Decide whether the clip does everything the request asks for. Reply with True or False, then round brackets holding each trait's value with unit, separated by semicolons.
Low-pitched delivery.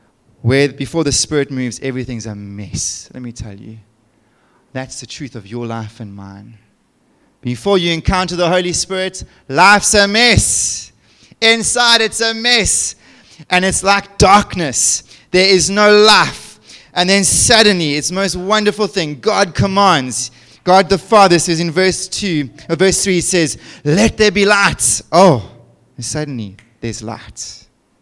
False (160 Hz)